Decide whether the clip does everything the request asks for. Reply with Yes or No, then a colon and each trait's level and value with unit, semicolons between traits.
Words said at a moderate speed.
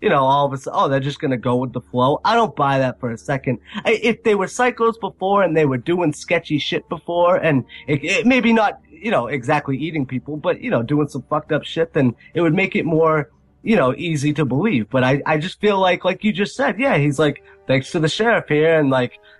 No: fast, 255 wpm